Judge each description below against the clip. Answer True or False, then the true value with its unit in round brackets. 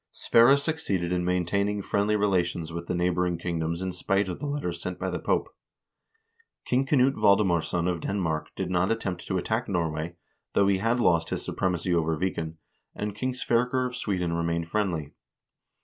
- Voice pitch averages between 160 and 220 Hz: False (90 Hz)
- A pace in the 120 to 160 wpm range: False (175 wpm)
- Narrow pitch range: False (3.7 semitones)